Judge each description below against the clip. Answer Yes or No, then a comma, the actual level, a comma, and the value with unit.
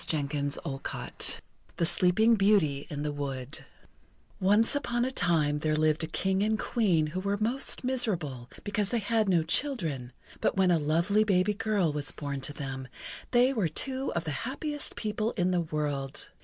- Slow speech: No, average, 170 wpm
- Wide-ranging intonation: Yes, wide, 6.4 semitones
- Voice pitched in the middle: Yes, medium, 180 Hz